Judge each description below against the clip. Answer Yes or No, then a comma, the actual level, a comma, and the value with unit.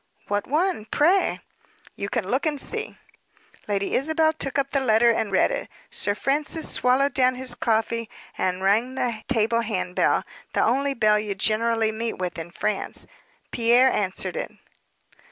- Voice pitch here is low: No, high, 230 Hz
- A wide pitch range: No, average, 4.4 semitones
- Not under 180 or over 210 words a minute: No, average, 160 wpm